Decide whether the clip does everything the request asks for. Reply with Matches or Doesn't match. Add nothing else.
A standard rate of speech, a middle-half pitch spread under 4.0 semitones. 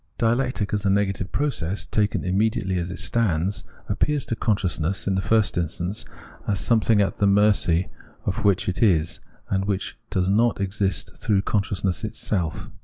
Matches